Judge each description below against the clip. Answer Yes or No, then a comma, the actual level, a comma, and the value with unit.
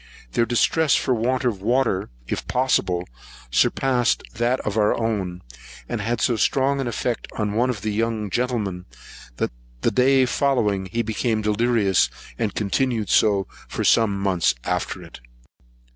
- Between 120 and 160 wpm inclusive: Yes, average, 150 wpm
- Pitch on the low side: Yes, low, 115 Hz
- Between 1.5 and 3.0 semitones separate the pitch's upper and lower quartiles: No, average, 3.5 semitones